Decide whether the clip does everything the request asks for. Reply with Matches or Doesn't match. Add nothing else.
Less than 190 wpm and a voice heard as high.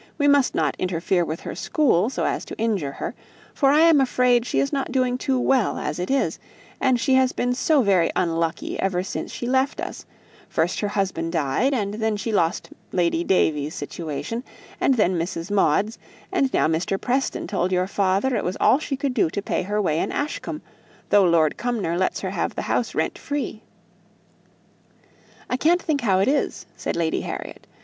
Doesn't match